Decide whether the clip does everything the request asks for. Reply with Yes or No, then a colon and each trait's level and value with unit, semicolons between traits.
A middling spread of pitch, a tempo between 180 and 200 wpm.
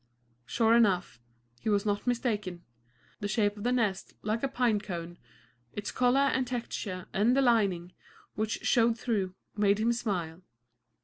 No: average, 3.6 semitones; average, 150 wpm